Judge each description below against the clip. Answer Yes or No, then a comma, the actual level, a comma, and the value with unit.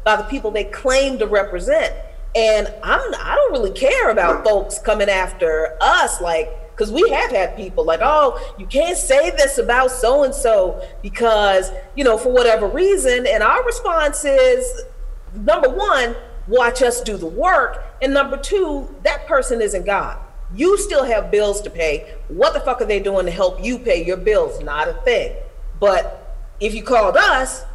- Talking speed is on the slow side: No, average, 185 wpm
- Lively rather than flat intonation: Yes, wide, 7.6 semitones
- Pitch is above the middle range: Yes, very high, 250 Hz